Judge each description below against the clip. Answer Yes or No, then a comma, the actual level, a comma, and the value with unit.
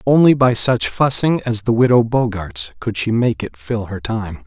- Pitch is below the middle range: Yes, low, 115 Hz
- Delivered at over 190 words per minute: Yes, average, 200 wpm